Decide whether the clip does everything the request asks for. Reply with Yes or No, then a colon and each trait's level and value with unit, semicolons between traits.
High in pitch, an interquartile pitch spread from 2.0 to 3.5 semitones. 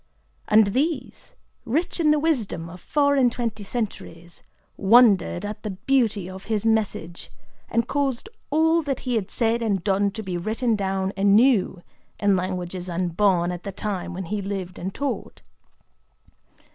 No: high, 205 Hz; average, 4.4 semitones